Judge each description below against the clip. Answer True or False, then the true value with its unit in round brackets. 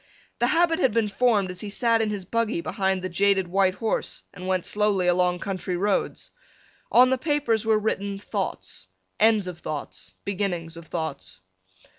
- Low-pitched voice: False (200 Hz)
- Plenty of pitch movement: False (3.6 semitones)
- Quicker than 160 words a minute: True (170 wpm)